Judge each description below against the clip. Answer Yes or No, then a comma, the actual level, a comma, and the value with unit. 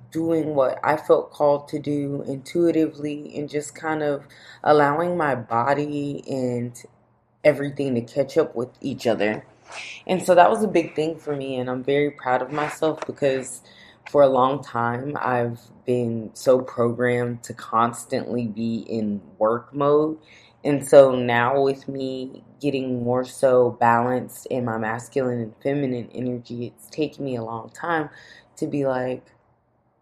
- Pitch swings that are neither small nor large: Yes, average, 3.3 semitones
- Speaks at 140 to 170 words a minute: Yes, average, 155 wpm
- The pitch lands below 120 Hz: No, low, 130 Hz